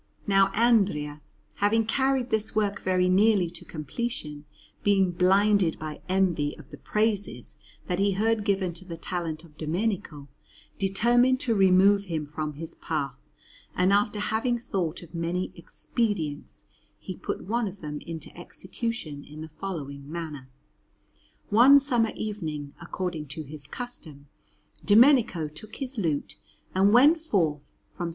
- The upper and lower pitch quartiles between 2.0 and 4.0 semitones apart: No, wide, 5.5 semitones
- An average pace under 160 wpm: Yes, average, 145 wpm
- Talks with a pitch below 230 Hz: Yes, medium, 185 Hz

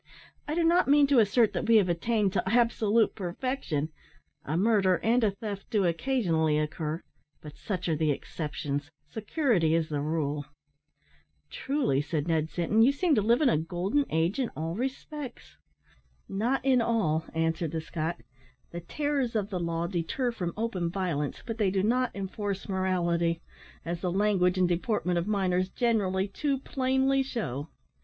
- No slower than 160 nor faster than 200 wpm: Yes, average, 165 wpm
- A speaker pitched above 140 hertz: Yes, high, 190 Hz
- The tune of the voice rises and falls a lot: Yes, wide, 6.0 semitones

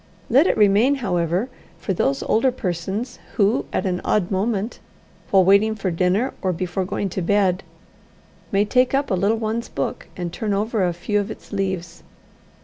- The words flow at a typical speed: Yes, average, 175 wpm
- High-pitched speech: Yes, high, 200 Hz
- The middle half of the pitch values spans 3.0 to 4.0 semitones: Yes, average, 3.3 semitones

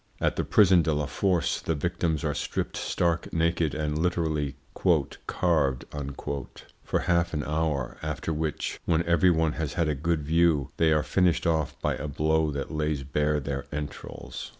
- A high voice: No, very low, 80 Hz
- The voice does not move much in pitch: Yes, narrow, 2.3 semitones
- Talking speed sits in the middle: Yes, average, 170 wpm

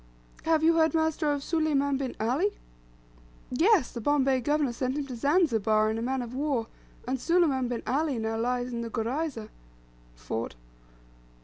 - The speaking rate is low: No, average, 165 wpm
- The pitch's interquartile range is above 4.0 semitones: Yes, average, 4.6 semitones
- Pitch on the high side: Yes, very high, 265 Hz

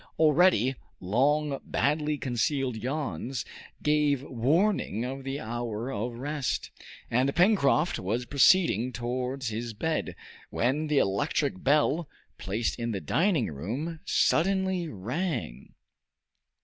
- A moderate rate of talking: No, slow, 110 wpm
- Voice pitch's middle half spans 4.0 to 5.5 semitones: Yes, average, 4.5 semitones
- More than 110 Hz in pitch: Yes, low, 135 Hz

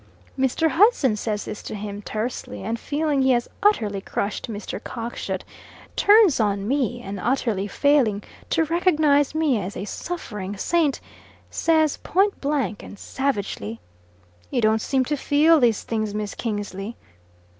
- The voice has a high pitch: Yes, high, 240 Hz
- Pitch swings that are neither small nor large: No, wide, 6.2 semitones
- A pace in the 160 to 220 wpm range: No, average, 145 wpm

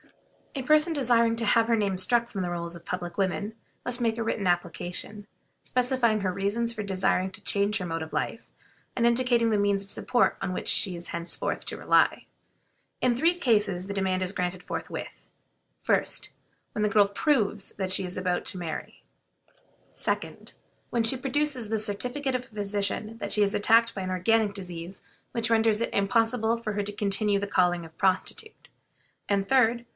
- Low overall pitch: No, high, 205 Hz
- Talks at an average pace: Yes, average, 190 wpm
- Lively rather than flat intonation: No, average, 3.7 semitones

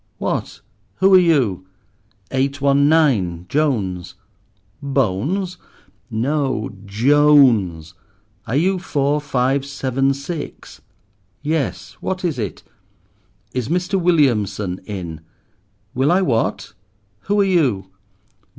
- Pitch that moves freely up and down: Yes, wide, 6.8 semitones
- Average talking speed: No, slow, 95 wpm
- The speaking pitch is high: No, low, 135 Hz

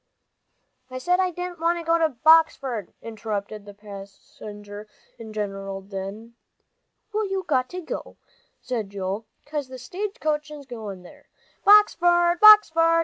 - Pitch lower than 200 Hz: No, very high, 255 Hz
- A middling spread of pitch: No, wide, 8.9 semitones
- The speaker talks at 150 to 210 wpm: No, average, 140 wpm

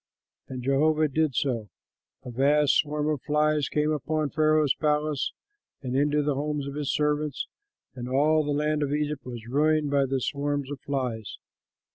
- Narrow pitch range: Yes, narrow, 1.8 semitones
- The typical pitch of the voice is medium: Yes, medium, 145 Hz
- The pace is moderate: Yes, average, 170 wpm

